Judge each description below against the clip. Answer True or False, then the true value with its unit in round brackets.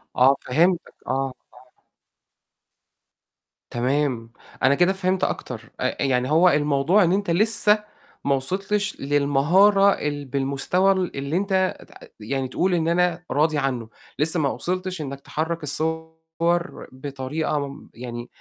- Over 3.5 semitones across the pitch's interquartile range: True (4.8 semitones)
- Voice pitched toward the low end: False (155 Hz)